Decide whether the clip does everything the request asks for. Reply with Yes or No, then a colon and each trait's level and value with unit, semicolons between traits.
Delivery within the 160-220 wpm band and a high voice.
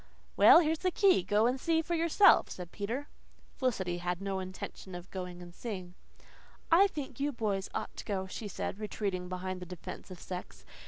Yes: average, 190 wpm; high, 195 Hz